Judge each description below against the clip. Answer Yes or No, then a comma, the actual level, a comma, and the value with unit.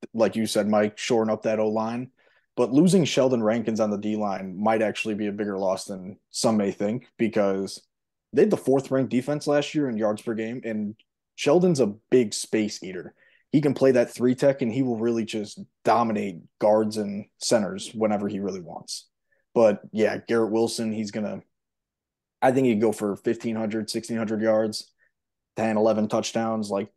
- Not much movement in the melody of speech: Yes, narrow, 2.1 semitones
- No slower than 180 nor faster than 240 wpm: Yes, average, 185 wpm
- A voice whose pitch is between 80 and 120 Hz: Yes, low, 110 Hz